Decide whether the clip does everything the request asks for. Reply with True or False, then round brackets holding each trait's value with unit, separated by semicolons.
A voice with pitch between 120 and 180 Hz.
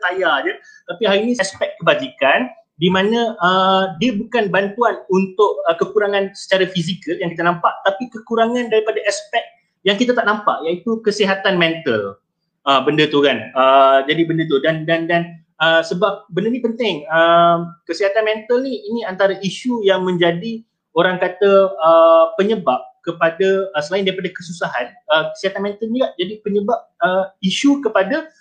False (195 Hz)